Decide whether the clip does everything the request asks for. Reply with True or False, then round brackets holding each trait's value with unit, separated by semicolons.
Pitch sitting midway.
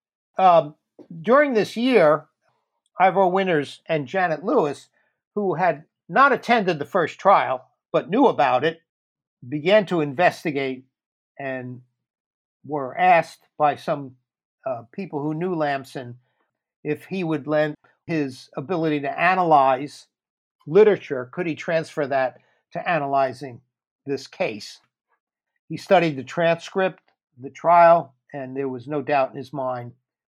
True (150 Hz)